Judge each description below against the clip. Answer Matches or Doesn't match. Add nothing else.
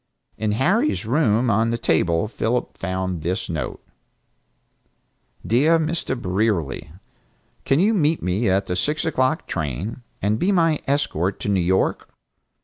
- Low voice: Matches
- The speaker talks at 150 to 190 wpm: Doesn't match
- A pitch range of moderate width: Doesn't match